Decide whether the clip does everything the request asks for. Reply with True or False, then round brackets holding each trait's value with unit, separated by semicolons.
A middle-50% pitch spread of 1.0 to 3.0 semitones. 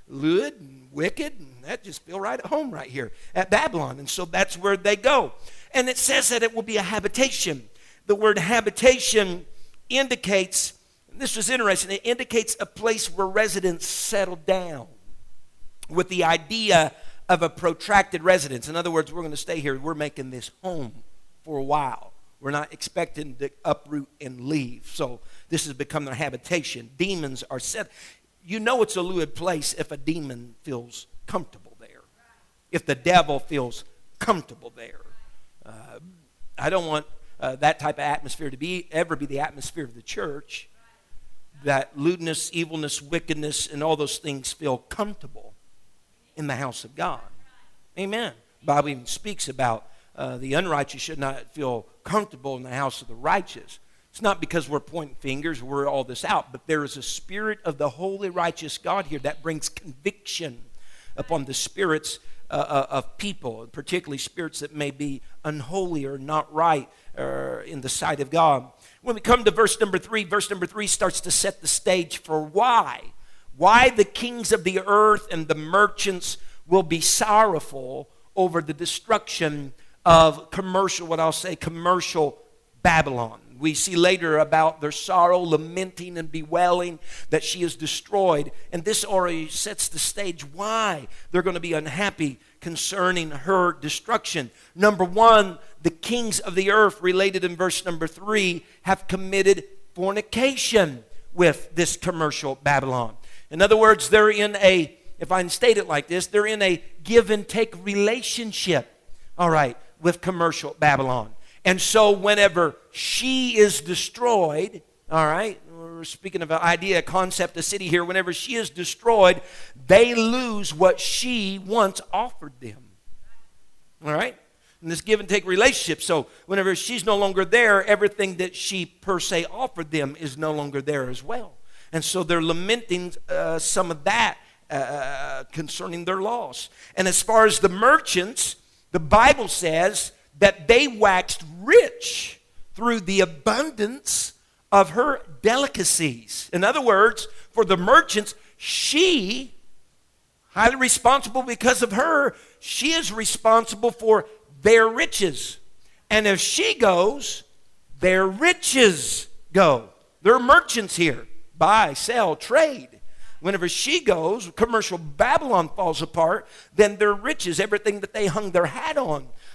False (5.6 semitones)